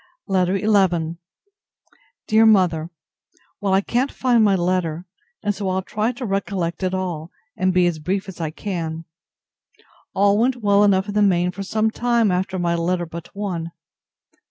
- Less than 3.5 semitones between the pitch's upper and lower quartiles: Yes, average, 2.9 semitones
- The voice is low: No, high, 190 Hz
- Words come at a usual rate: Yes, average, 165 wpm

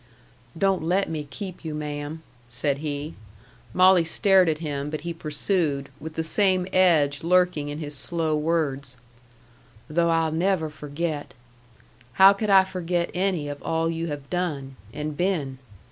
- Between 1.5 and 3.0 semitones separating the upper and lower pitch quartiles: No, average, 3.5 semitones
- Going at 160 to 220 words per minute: No, average, 150 wpm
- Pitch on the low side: No, medium, 160 Hz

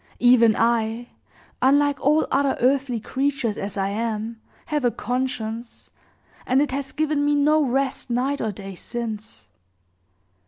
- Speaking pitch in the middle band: No, very high, 250 Hz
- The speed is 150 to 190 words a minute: No, average, 140 wpm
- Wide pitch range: No, average, 3.8 semitones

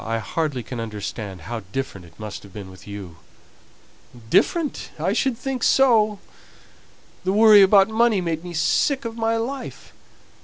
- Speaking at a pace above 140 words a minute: Yes, average, 155 wpm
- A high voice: No, medium, 175 Hz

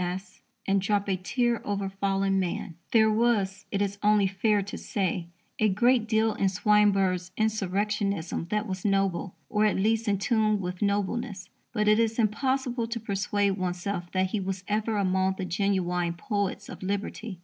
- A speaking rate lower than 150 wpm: No, average, 170 wpm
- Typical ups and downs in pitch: No, narrow, 2.2 semitones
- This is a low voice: No, high, 200 Hz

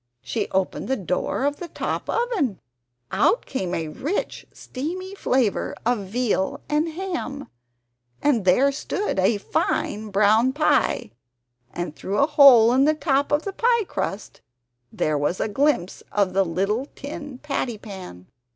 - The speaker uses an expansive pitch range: Yes, wide, 7.2 semitones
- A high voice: Yes, very high, 255 Hz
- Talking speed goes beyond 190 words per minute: No, average, 150 wpm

